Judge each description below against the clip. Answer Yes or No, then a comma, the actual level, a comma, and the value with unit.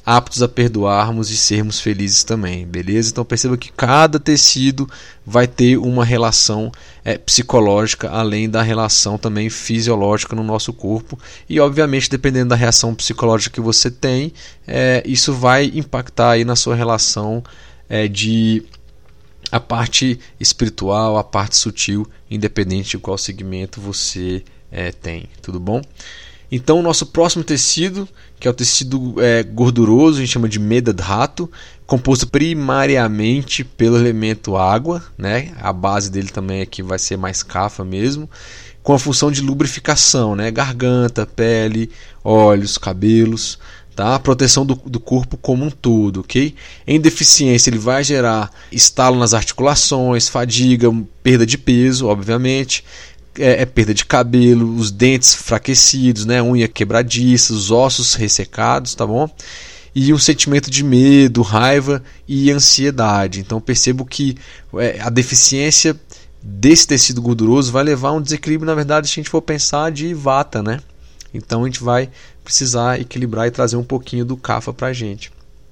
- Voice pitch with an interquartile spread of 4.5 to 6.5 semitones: No, average, 3.7 semitones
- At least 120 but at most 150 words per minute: Yes, average, 145 wpm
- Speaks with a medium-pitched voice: No, low, 120 Hz